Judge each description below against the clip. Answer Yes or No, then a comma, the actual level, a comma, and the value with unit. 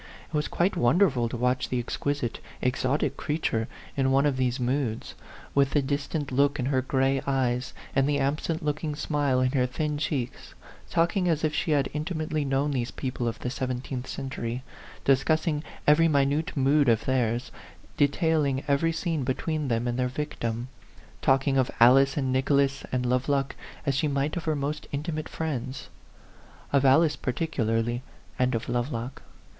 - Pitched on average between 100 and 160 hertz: Yes, low, 135 Hz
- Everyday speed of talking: Yes, average, 175 wpm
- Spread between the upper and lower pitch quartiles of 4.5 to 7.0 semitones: No, average, 2.9 semitones